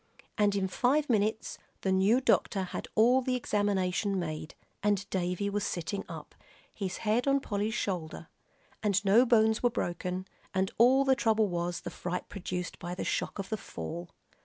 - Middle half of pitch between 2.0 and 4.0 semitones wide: Yes, average, 3.5 semitones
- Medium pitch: No, high, 200 Hz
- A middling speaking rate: Yes, average, 170 wpm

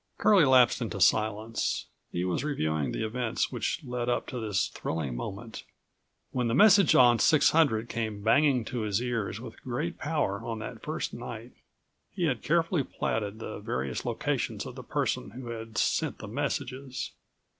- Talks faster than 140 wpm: Yes, average, 165 wpm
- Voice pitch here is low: Yes, low, 120 Hz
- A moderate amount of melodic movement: Yes, average, 3.9 semitones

